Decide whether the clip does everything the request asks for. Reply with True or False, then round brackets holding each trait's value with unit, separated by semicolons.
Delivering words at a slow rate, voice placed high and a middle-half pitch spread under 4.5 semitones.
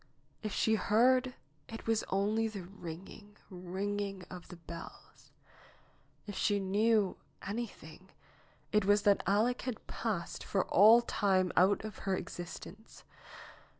True (125 wpm; 205 Hz; 2.7 semitones)